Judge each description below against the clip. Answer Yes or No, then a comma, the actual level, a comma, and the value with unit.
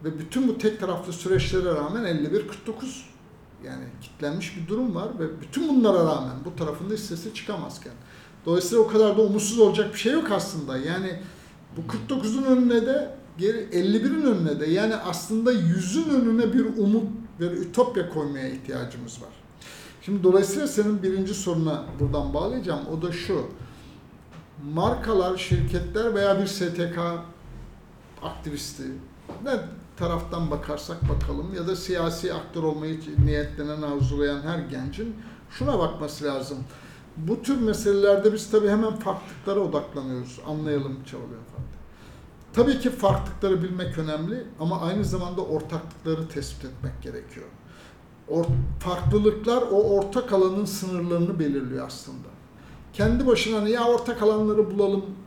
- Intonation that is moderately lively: No, wide, 5.8 semitones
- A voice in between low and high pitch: Yes, medium, 180 Hz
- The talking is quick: No, average, 130 wpm